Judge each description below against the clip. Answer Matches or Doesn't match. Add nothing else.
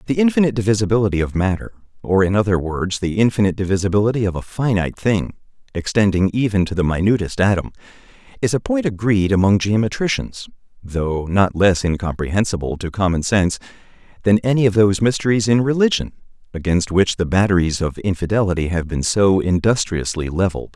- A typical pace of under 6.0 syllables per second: Doesn't match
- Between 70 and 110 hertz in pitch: Matches